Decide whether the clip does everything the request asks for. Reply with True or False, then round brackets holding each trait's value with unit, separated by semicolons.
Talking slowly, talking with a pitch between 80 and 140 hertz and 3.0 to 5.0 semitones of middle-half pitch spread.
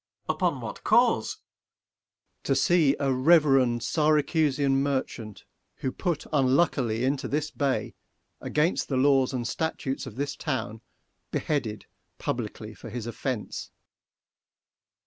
True (125 wpm; 135 Hz; 3.6 semitones)